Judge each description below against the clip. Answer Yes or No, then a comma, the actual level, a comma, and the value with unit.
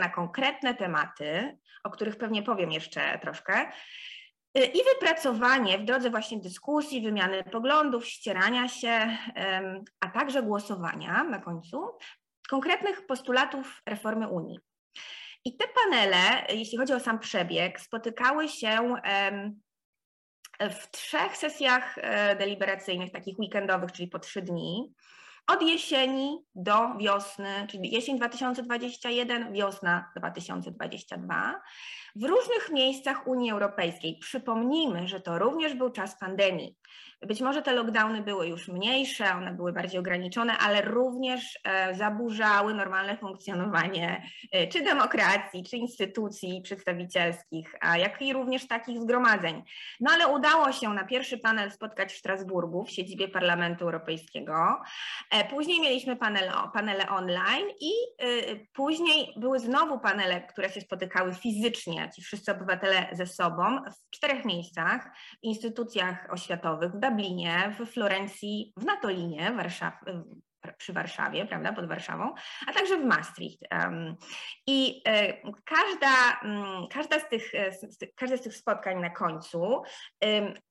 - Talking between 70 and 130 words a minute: Yes, average, 125 wpm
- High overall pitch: Yes, high, 215 Hz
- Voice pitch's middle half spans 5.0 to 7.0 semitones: Yes, wide, 5.4 semitones